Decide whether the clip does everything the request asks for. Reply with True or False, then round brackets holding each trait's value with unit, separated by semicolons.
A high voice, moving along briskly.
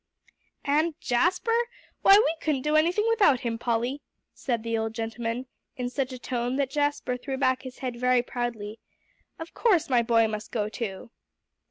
False (250 Hz; 170 wpm)